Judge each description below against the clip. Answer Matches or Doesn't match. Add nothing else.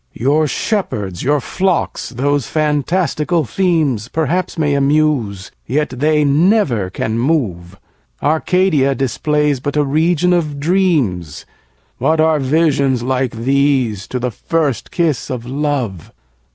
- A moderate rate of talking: Doesn't match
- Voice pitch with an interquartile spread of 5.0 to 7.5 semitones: Doesn't match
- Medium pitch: Matches